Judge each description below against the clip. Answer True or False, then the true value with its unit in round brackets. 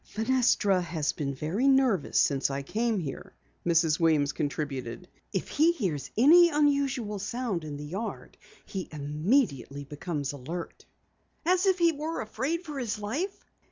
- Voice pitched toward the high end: True (195 Hz)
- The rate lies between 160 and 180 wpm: False (145 wpm)